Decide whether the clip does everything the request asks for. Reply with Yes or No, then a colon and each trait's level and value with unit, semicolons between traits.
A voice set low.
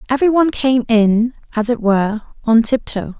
No: high, 235 Hz